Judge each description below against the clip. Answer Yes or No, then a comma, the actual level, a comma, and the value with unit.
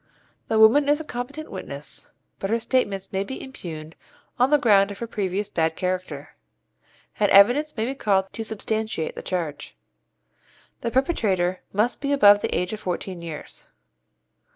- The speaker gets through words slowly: No, average, 160 wpm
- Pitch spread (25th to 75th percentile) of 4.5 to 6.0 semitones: Yes, average, 4.9 semitones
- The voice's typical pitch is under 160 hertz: No, high, 205 Hz